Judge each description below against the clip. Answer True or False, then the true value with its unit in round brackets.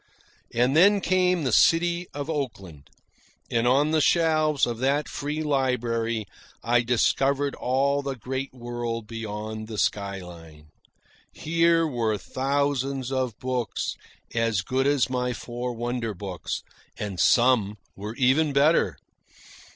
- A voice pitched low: True (125 Hz)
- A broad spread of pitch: False (4.0 semitones)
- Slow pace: True (125 wpm)